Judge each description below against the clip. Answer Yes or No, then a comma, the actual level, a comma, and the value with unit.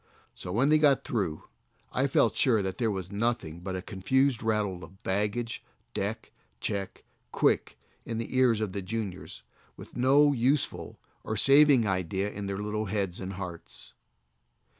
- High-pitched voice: No, low, 105 Hz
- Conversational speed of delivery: Yes, average, 160 wpm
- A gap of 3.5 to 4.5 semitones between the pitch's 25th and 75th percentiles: Yes, average, 4.1 semitones